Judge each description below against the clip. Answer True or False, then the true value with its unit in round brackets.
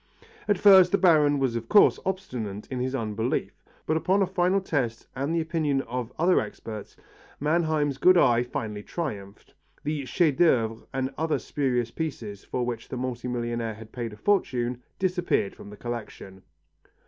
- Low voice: True (130 Hz)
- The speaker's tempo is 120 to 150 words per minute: False (165 wpm)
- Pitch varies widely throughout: True (5.9 semitones)